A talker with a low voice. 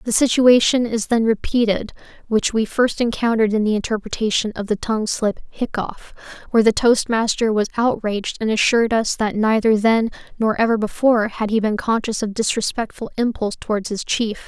No: high, 220 Hz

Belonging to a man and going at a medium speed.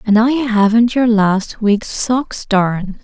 No: female; average, 160 wpm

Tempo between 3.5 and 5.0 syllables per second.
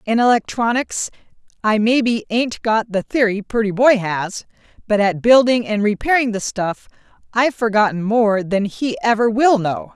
Yes: 4.6 syllables/s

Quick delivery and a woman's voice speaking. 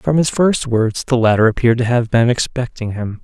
No: fast, 225 wpm; male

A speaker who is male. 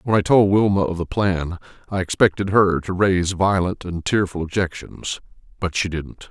Yes: male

